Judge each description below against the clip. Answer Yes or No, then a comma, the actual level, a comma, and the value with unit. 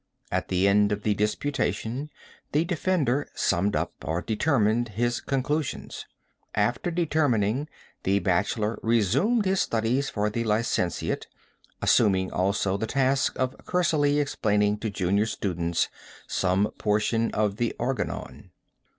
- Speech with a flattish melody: No, average, 5.1 semitones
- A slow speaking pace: Yes, slow, 125 wpm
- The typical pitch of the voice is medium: No, low, 110 Hz